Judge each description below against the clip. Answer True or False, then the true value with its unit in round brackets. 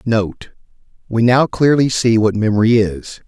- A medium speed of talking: False (130 wpm)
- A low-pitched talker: True (115 Hz)